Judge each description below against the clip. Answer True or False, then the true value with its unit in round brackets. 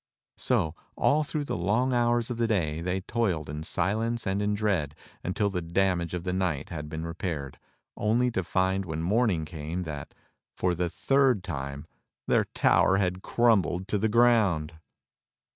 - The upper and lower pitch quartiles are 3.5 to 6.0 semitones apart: True (5.1 semitones)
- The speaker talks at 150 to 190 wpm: True (165 wpm)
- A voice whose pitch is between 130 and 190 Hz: False (95 Hz)